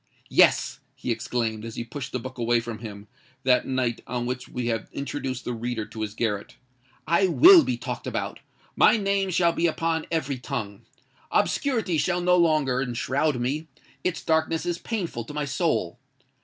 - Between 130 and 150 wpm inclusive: No, average, 170 wpm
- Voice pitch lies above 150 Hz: No, low, 130 Hz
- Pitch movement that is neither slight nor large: No, wide, 5.9 semitones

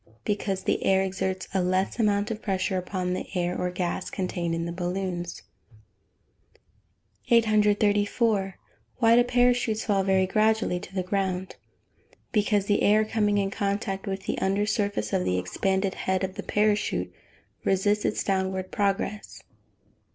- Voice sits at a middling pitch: No, high, 195 Hz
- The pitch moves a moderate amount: No, narrow, 2.0 semitones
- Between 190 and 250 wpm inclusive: No, average, 150 wpm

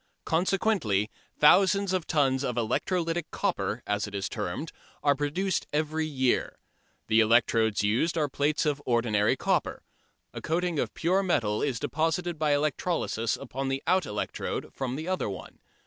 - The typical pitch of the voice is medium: Yes, medium, 145 Hz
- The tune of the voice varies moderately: No, wide, 6.5 semitones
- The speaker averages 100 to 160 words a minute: Yes, average, 150 wpm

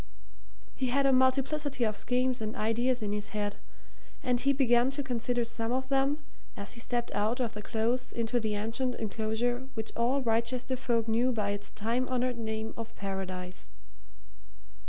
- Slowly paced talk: No, average, 170 wpm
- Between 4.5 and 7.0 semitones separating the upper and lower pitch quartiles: No, average, 2.7 semitones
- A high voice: Yes, high, 235 Hz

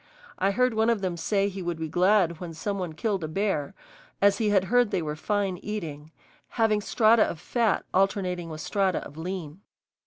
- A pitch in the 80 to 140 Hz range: No, high, 190 Hz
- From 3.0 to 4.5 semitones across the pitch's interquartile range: Yes, average, 3.9 semitones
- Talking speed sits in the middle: Yes, average, 195 wpm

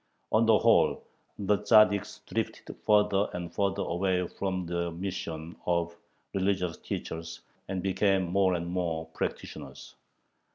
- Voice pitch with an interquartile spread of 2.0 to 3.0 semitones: Yes, narrow, 2.4 semitones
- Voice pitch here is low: Yes, very low, 95 Hz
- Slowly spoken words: Yes, slow, 125 wpm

